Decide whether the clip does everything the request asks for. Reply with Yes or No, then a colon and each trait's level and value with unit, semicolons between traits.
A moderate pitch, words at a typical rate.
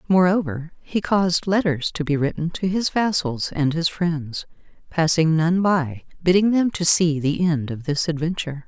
Yes: medium, 165 Hz; average, 160 wpm